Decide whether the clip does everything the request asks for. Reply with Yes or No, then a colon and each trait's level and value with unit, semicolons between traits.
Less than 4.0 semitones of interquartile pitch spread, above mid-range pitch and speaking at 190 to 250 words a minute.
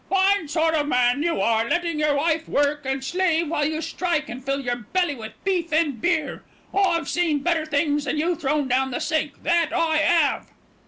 Yes: average, 3.2 semitones; very high, 310 Hz; average, 200 wpm